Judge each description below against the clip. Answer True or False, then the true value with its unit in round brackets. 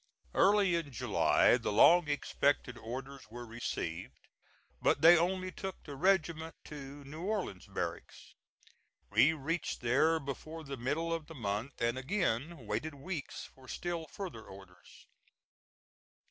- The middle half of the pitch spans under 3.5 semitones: False (5.2 semitones)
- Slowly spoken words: True (130 wpm)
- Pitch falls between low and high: True (145 Hz)